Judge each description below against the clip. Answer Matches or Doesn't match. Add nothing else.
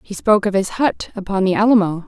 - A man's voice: Doesn't match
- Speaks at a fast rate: Matches